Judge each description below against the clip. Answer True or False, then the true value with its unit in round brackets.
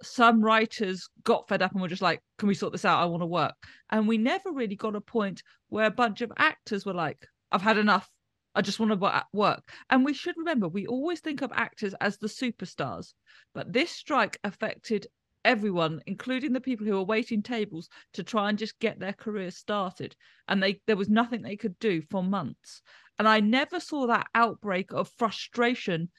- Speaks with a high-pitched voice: True (215 Hz)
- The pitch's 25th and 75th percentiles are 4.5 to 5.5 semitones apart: False (3.1 semitones)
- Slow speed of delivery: False (205 wpm)